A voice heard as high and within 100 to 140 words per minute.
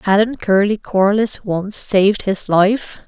Yes: high, 205 Hz; slow, 135 wpm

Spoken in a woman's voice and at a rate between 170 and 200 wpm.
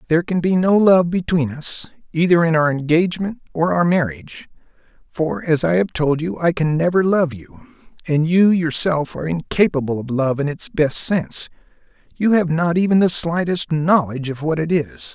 No: male; average, 185 wpm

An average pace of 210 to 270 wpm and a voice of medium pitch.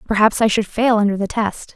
No: fast, 240 wpm; high, 215 Hz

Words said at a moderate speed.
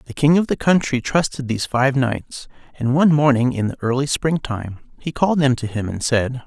No: fast, 225 wpm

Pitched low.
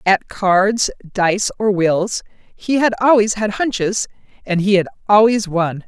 No: high, 200 Hz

